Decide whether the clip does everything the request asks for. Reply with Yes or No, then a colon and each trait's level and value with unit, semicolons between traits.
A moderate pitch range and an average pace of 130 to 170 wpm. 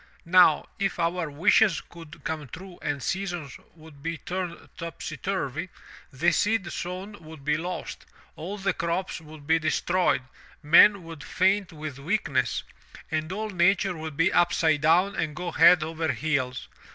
Yes: average, 3.0 semitones; average, 150 wpm